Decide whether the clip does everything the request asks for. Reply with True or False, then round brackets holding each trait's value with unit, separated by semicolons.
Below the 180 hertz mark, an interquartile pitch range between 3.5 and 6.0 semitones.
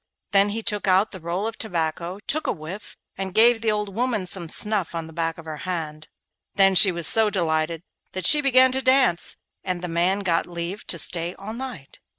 False (185 Hz; 4.3 semitones)